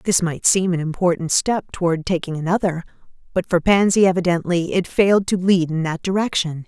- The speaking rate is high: No, average, 180 wpm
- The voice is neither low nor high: Yes, medium, 175 Hz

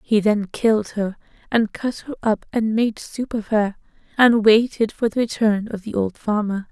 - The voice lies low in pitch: No, high, 215 Hz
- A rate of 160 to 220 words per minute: Yes, average, 195 wpm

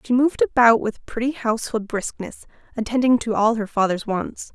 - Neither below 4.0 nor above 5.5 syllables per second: Yes, 5.4 syllables/s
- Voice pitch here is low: No, high, 230 Hz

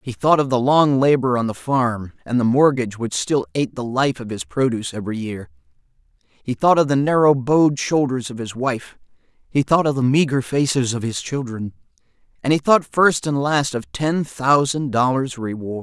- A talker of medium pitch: No, low, 130 Hz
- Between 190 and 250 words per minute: Yes, average, 195 wpm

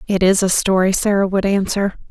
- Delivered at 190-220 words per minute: Yes, average, 200 wpm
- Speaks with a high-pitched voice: Yes, high, 195 Hz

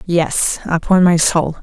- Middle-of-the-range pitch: Yes, medium, 170 Hz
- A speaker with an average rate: Yes, average, 145 wpm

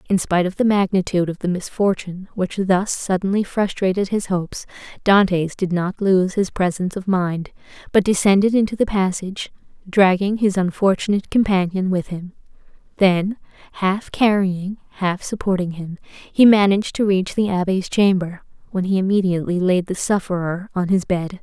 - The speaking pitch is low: No, high, 190 Hz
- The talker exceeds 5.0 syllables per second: Yes, 5.2 syllables/s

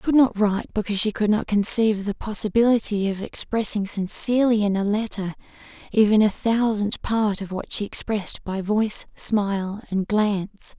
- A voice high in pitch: Yes, high, 210 Hz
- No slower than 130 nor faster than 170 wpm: Yes, average, 165 wpm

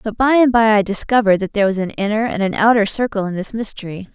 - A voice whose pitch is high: Yes, high, 210 Hz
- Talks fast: Yes, fast, 260 wpm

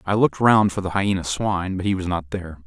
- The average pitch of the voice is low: Yes, very low, 95 Hz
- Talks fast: Yes, fast, 270 wpm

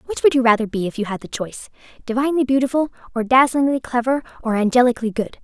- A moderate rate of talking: Yes, average, 190 wpm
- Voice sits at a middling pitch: No, high, 245 Hz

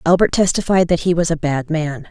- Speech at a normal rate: No, fast, 230 wpm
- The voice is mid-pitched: Yes, medium, 165 Hz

